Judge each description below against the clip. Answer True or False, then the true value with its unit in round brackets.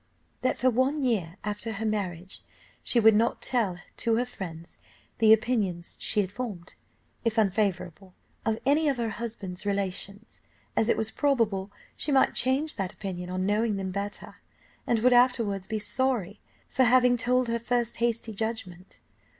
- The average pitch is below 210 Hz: False (220 Hz)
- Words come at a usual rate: True (160 wpm)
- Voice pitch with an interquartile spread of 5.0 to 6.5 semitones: False (3.8 semitones)